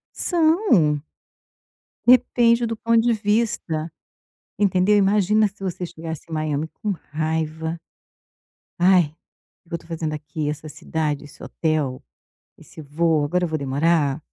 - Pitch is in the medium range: Yes, medium, 165 Hz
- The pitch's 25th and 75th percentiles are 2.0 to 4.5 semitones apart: No, average, 5.1 semitones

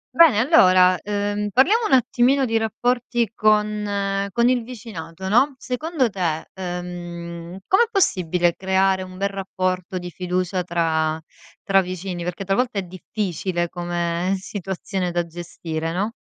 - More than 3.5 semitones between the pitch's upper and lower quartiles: Yes, average, 3.9 semitones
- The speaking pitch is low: No, high, 190 Hz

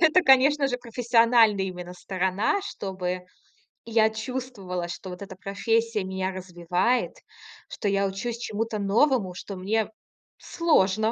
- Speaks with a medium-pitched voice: No, high, 210 Hz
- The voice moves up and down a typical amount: Yes, average, 4.0 semitones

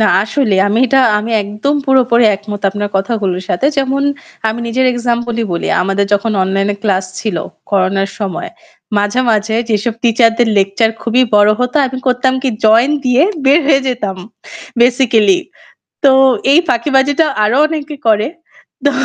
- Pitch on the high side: Yes, high, 230 Hz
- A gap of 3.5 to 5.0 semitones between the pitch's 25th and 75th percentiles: Yes, average, 4.0 semitones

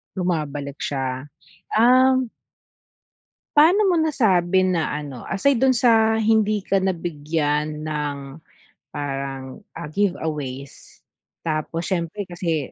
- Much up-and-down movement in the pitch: Yes, wide, 6.8 semitones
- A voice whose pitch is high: No, medium, 170 Hz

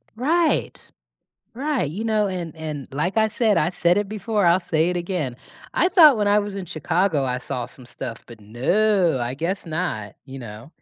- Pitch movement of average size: No, wide, 7.2 semitones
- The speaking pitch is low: No, medium, 175 Hz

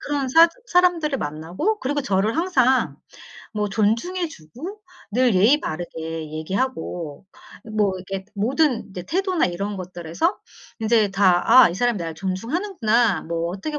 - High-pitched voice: Yes, high, 215 Hz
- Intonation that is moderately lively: No, wide, 8.3 semitones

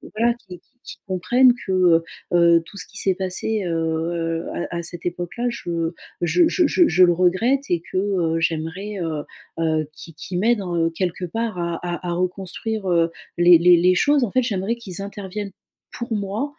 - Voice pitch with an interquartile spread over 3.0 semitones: Yes, average, 3.7 semitones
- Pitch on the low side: No, medium, 180 Hz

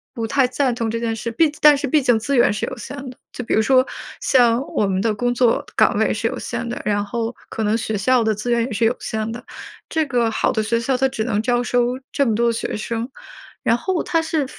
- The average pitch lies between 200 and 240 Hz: Yes, high, 235 Hz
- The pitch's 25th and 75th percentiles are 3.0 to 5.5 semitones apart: No, narrow, 2.4 semitones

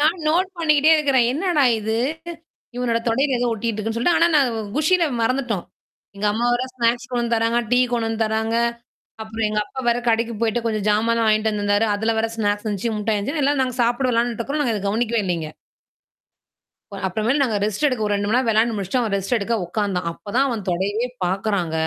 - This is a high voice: Yes, high, 230 Hz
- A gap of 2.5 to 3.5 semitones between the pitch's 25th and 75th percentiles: Yes, average, 2.9 semitones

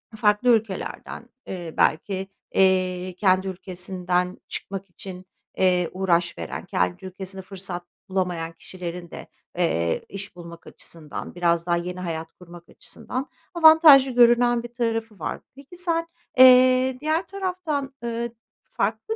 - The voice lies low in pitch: No, high, 190 Hz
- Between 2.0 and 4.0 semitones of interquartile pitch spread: No, wide, 5.4 semitones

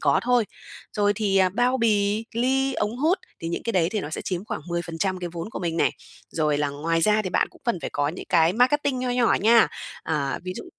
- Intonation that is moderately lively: No, wide, 6.0 semitones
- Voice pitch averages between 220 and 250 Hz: No, high, 200 Hz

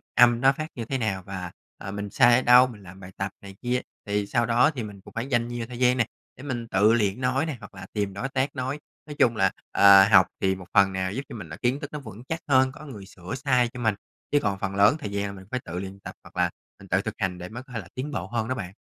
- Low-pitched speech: Yes, low, 110 Hz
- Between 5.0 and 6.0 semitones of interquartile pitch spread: No, average, 4.6 semitones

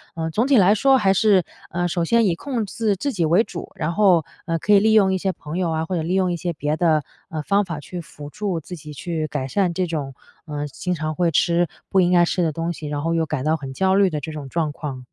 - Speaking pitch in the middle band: Yes, medium, 170 Hz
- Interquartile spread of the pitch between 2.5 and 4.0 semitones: Yes, average, 3.6 semitones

